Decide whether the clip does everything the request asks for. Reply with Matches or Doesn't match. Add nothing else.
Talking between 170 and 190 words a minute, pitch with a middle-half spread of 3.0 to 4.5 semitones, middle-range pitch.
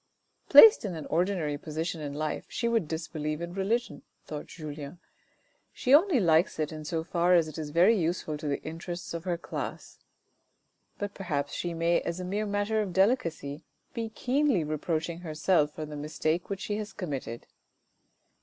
Matches